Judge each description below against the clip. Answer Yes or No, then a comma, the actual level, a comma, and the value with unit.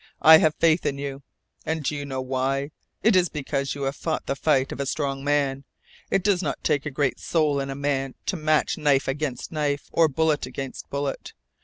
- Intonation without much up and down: Yes, narrow, 2.2 semitones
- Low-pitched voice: No, medium, 145 Hz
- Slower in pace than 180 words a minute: No, fast, 205 wpm